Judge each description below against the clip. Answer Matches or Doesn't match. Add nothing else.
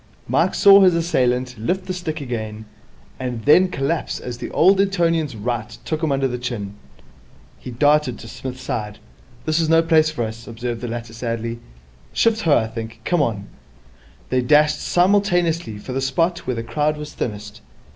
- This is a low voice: Matches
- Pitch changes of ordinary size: Doesn't match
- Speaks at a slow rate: Doesn't match